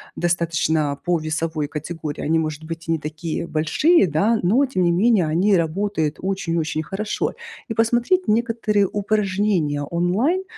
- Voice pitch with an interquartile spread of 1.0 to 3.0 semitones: No, average, 5.0 semitones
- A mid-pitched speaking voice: Yes, medium, 175 Hz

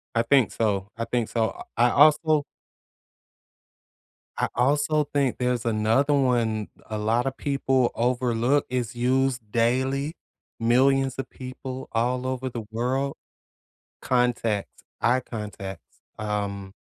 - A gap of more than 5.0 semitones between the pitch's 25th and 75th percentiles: No, average, 2.8 semitones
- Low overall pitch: Yes, low, 125 Hz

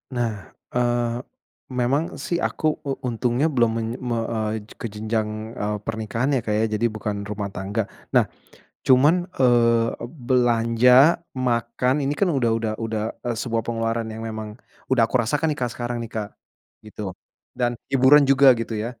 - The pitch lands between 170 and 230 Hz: No, low, 115 Hz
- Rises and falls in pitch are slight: Yes, narrow, 2.0 semitones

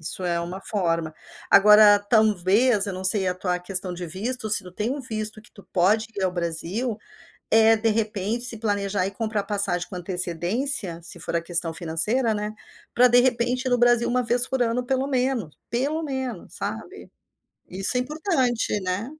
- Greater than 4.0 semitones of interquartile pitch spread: Yes, average, 4.8 semitones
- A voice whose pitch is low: No, high, 210 Hz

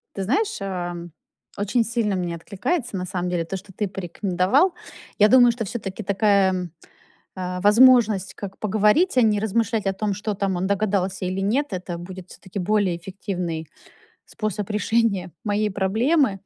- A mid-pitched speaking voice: No, high, 200 Hz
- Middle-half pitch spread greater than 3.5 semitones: No, average, 2.9 semitones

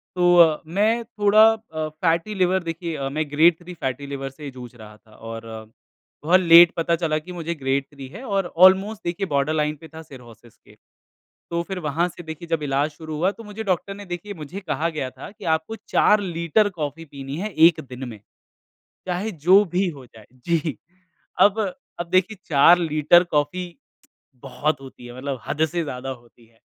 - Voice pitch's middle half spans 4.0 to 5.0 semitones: Yes, average, 4.6 semitones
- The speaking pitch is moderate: Yes, medium, 165 Hz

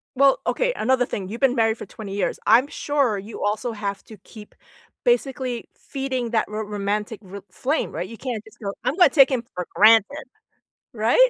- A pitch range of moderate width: Yes, average, 4.1 semitones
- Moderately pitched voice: No, high, 225 Hz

